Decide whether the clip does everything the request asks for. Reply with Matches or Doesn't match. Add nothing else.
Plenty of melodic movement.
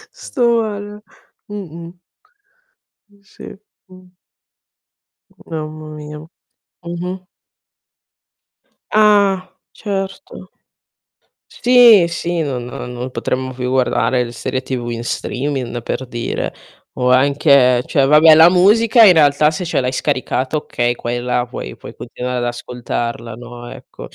Matches